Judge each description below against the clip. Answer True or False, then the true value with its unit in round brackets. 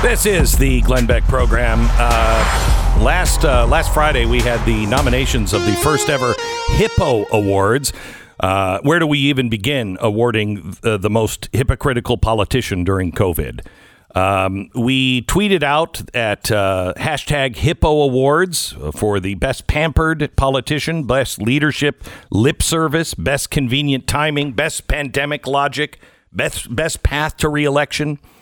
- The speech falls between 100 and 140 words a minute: True (135 wpm)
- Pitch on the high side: False (130 Hz)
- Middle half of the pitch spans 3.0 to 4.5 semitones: False (5.2 semitones)